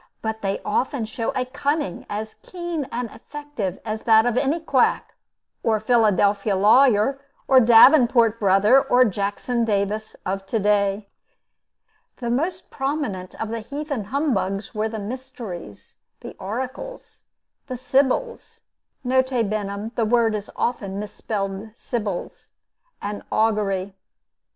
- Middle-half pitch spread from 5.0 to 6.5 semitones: No, average, 4.1 semitones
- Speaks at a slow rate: Yes, slow, 125 wpm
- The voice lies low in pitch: No, high, 220 Hz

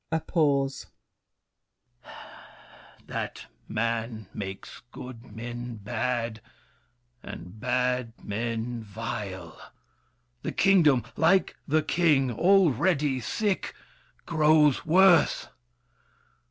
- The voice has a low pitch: Yes, low, 125 Hz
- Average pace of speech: No, slow, 75 wpm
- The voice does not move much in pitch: No, wide, 5.5 semitones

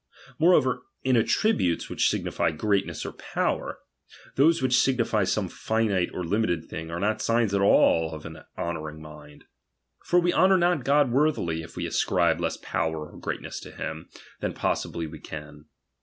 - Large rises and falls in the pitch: Yes, wide, 8.3 semitones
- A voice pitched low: Yes, low, 100 Hz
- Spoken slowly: No, average, 165 wpm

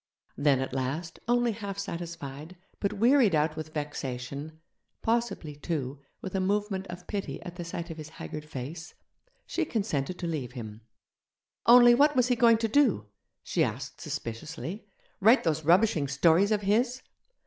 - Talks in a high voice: No, medium, 170 Hz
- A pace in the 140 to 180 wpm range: Yes, average, 160 wpm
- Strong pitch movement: Yes, wide, 6.4 semitones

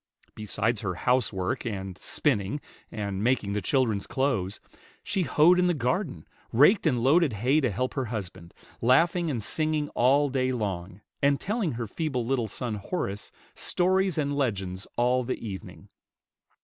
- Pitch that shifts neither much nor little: No, wide, 6.2 semitones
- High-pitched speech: No, low, 125 Hz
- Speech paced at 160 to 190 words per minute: No, average, 150 wpm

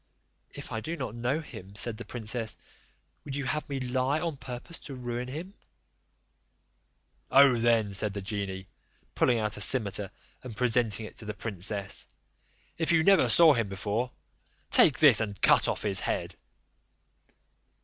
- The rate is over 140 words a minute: Yes, average, 160 wpm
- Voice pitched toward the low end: Yes, low, 120 Hz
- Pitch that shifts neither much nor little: Yes, average, 4.4 semitones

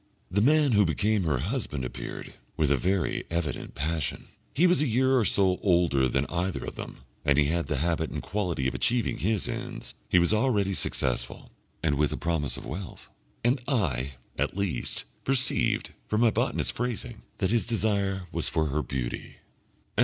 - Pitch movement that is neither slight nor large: No, wide, 6.6 semitones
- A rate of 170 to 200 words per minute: Yes, average, 180 wpm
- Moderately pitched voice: No, very low, 90 Hz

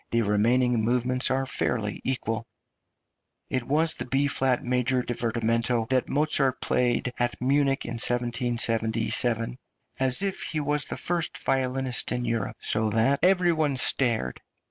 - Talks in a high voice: No, low, 125 Hz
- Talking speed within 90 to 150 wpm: Yes, average, 140 wpm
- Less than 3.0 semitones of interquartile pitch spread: Yes, narrow, 2.5 semitones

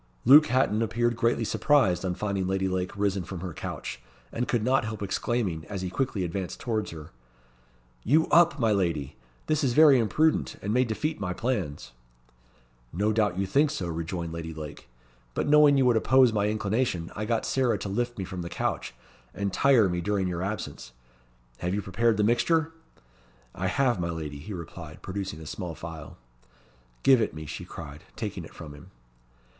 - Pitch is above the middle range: No, low, 100 Hz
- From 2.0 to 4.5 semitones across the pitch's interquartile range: No, wide, 5.4 semitones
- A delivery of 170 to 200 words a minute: Yes, average, 185 wpm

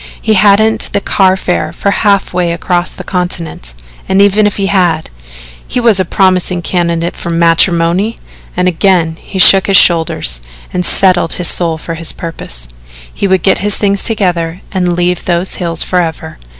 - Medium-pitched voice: Yes, medium, 180 Hz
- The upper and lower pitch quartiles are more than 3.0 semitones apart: No, narrow, 2.5 semitones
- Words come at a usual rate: Yes, average, 170 wpm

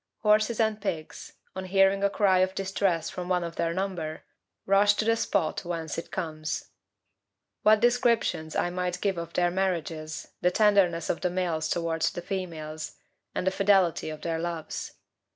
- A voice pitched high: No, medium, 180 Hz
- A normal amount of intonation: Yes, average, 3.0 semitones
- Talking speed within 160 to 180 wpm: Yes, average, 170 wpm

